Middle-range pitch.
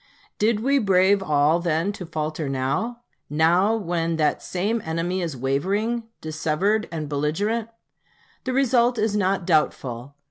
Yes: medium, 180 Hz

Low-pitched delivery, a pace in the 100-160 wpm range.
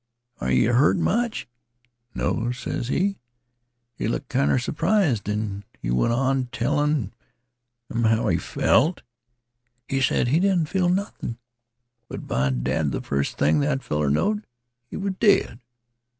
Yes: low, 125 Hz; average, 140 wpm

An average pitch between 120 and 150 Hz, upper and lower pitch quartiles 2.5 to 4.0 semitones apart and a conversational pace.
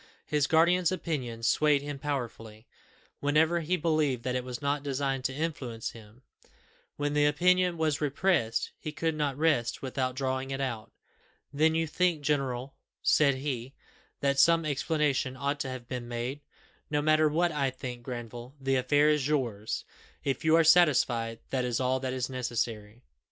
Yes: medium, 140 Hz; average, 3.3 semitones; average, 165 wpm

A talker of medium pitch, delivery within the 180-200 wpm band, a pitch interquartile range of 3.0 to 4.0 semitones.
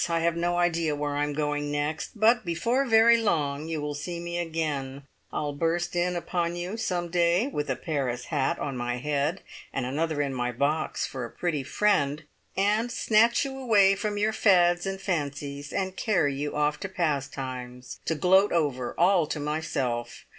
No: medium, 160 Hz; average, 185 wpm; average, 4.4 semitones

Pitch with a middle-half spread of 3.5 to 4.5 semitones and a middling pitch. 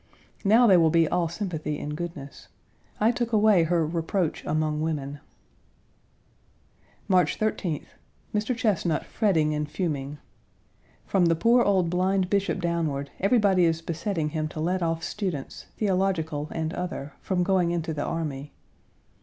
Yes: average, 3.8 semitones; medium, 170 Hz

